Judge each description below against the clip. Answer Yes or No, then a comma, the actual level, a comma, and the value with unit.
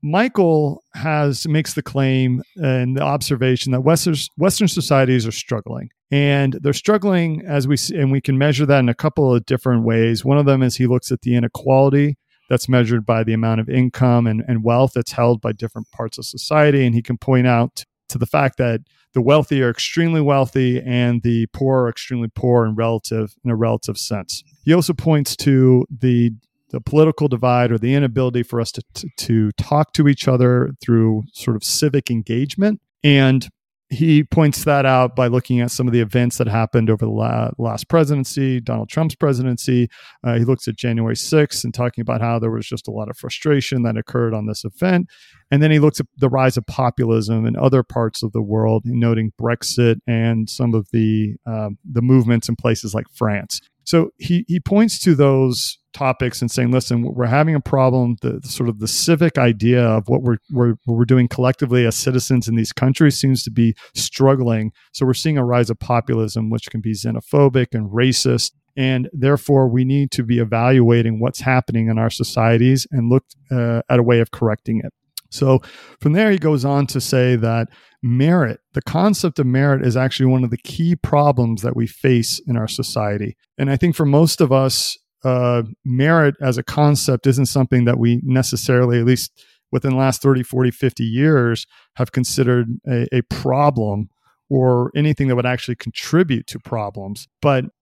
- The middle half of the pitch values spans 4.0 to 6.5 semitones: No, average, 3.0 semitones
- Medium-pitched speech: No, low, 125 Hz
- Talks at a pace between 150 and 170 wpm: No, average, 195 wpm